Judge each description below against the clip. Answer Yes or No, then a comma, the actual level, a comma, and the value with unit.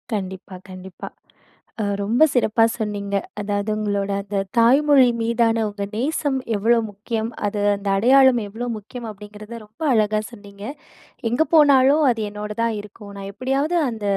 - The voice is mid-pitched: No, high, 215 Hz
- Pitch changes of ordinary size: Yes, average, 3.2 semitones